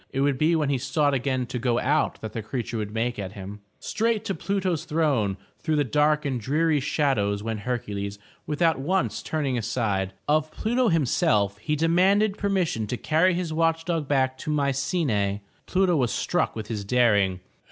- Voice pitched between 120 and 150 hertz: Yes, medium, 140 Hz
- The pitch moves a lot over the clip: Yes, wide, 6.6 semitones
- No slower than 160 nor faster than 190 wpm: Yes, average, 185 wpm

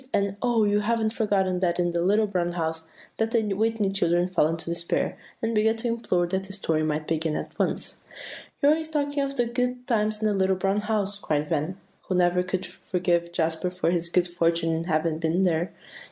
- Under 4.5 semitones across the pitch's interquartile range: Yes, average, 4.0 semitones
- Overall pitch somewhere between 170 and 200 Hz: Yes, medium, 185 Hz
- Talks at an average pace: No, fast, 210 wpm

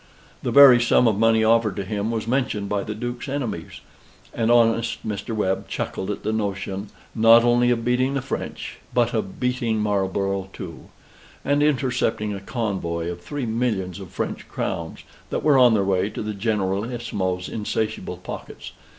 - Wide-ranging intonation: No, average, 3.6 semitones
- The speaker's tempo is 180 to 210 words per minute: No, average, 165 wpm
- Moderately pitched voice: No, low, 110 Hz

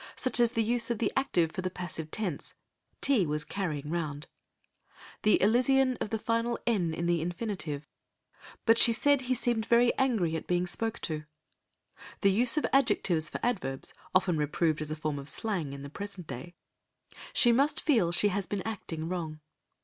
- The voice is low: No, high, 190 Hz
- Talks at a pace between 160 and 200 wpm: Yes, average, 180 wpm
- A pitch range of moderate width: No, wide, 6.5 semitones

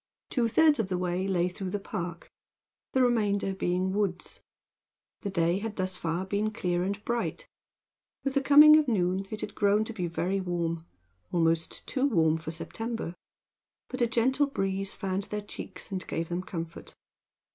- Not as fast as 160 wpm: No, average, 170 wpm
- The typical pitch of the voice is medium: No, high, 195 Hz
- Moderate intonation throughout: Yes, average, 4.1 semitones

